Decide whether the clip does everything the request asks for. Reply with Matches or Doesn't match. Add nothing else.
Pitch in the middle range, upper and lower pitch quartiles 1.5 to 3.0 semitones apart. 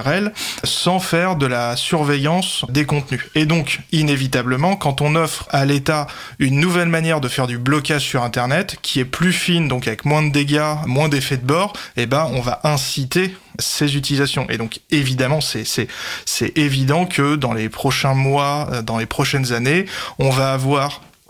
Matches